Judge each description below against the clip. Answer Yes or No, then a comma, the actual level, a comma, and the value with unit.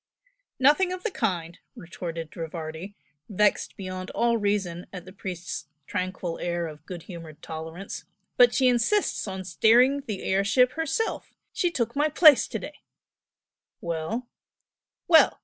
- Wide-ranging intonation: Yes, wide, 6.6 semitones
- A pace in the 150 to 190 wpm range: No, average, 140 wpm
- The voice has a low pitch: No, high, 195 Hz